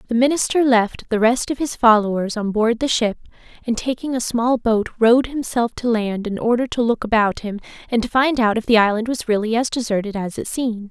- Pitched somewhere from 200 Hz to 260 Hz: Yes, high, 230 Hz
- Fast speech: Yes, fast, 225 wpm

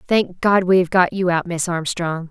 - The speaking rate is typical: No, fast, 235 wpm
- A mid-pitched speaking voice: Yes, medium, 180 Hz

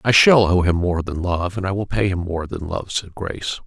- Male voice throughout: Yes, male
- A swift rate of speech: Yes, fast, 280 wpm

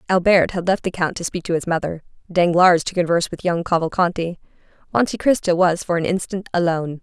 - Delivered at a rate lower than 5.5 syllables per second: No, 6.0 syllables/s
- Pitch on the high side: No, medium, 175 Hz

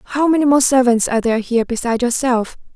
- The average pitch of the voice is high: Yes, very high, 250 Hz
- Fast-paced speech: No, average, 195 wpm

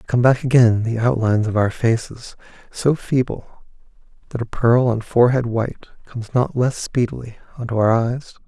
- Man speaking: Yes, male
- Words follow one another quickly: No, average, 165 wpm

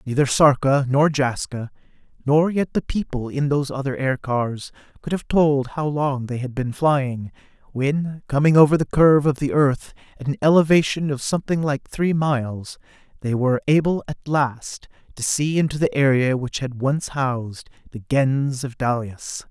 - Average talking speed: Yes, average, 170 wpm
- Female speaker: No, male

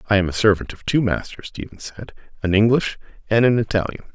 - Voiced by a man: Yes, male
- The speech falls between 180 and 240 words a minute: Yes, fast, 205 wpm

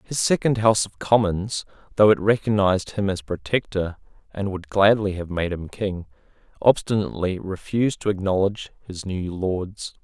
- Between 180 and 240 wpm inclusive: No, average, 150 wpm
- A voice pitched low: Yes, low, 100 Hz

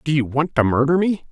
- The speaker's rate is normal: No, fast, 275 wpm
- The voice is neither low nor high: Yes, medium, 145 Hz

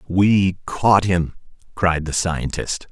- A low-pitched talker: Yes, very low, 90 Hz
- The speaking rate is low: Yes, slow, 125 wpm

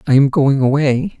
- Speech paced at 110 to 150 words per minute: No, average, 200 wpm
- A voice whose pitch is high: No, medium, 150 Hz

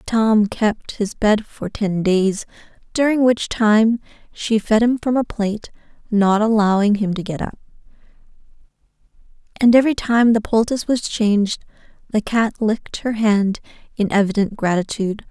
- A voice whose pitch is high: Yes, high, 215 Hz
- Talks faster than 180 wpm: No, average, 145 wpm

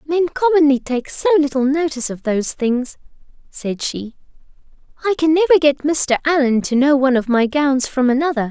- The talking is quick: No, average, 175 wpm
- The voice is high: Yes, very high, 280 Hz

